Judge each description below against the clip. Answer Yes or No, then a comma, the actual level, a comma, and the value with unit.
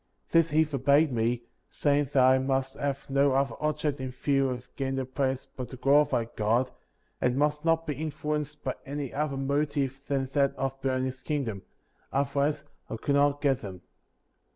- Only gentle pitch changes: Yes, narrow, 1.9 semitones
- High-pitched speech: No, medium, 140 Hz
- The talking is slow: No, average, 175 wpm